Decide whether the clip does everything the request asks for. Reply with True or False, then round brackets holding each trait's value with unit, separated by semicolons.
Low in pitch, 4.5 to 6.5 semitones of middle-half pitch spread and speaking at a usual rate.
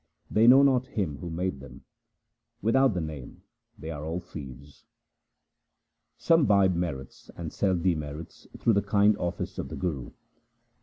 True (90 Hz; 5.5 semitones; 150 wpm)